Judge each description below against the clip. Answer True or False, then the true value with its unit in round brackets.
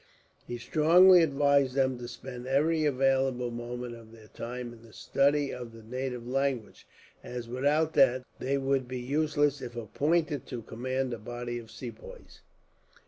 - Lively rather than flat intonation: False (2.9 semitones)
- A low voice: True (130 Hz)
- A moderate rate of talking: True (155 wpm)